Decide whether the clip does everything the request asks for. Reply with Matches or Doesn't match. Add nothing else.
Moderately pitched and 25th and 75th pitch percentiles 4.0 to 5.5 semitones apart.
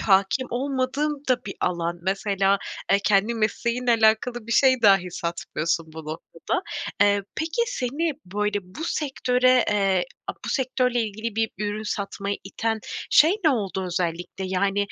Doesn't match